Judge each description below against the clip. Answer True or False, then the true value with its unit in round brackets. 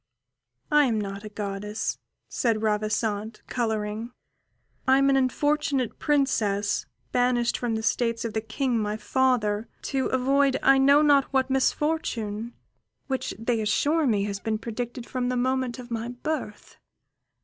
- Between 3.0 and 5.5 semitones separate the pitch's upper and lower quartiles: True (3.7 semitones)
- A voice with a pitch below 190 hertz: False (240 Hz)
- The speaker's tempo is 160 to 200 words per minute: False (145 wpm)